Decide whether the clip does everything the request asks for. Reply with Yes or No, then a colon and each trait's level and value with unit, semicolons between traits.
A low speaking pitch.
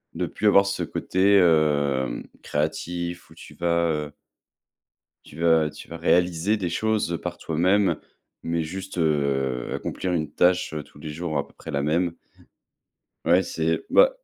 Yes: very low, 85 Hz